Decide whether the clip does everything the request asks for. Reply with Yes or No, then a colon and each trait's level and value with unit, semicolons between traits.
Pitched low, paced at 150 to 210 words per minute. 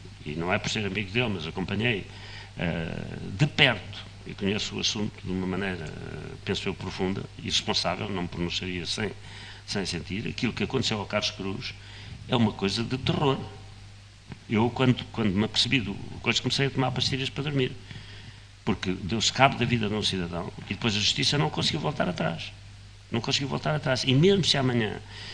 Yes: low, 105 Hz; average, 180 wpm